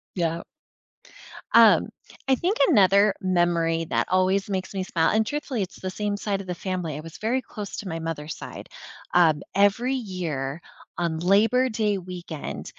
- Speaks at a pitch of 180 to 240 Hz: Yes, medium, 185 Hz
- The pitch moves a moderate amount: Yes, average, 3.7 semitones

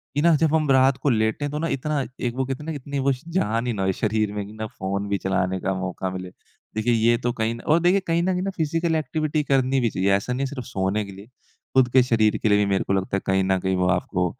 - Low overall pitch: Yes, low, 115 Hz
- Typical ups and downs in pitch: No, wide, 6.8 semitones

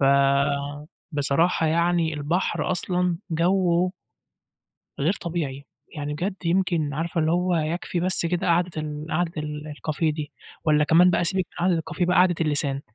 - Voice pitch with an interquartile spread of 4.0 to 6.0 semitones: No, average, 3.0 semitones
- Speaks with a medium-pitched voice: Yes, medium, 165 Hz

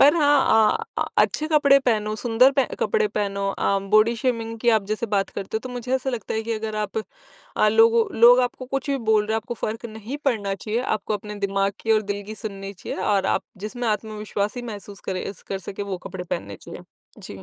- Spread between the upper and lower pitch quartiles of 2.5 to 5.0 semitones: Yes, average, 3.2 semitones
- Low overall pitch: No, high, 220 Hz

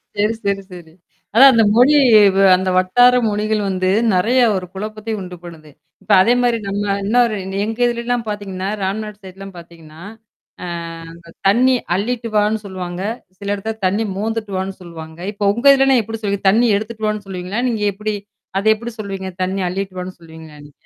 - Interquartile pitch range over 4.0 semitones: No, average, 3.2 semitones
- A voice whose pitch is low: No, high, 205 Hz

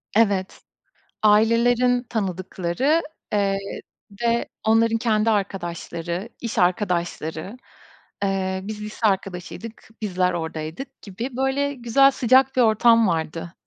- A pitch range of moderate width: Yes, average, 4.3 semitones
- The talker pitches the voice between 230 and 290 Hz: No, high, 210 Hz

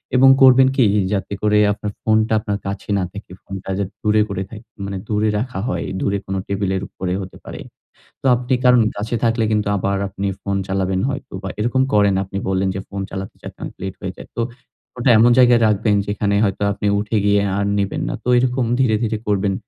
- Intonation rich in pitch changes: No, average, 2.8 semitones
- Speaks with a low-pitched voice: Yes, low, 105 Hz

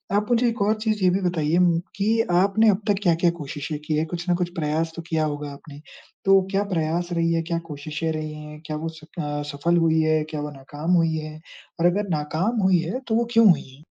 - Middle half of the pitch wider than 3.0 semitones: Yes, average, 3.8 semitones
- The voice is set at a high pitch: No, medium, 165 Hz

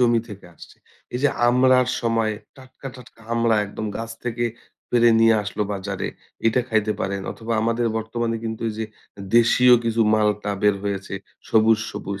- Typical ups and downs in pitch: No, narrow, 2.0 semitones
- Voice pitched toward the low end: Yes, low, 115 Hz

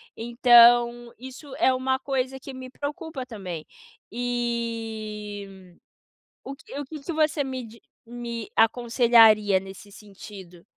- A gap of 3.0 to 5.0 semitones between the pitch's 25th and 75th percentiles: Yes, average, 3.5 semitones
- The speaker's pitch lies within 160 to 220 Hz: No, high, 240 Hz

